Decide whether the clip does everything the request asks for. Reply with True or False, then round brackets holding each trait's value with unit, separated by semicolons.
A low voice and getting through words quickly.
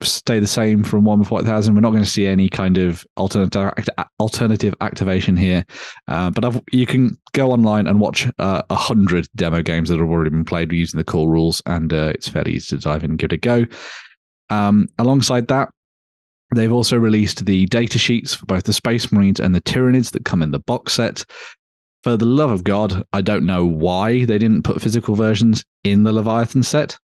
True (105 Hz; 210 wpm)